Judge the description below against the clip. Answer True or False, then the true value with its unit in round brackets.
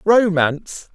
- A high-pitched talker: False (180 Hz)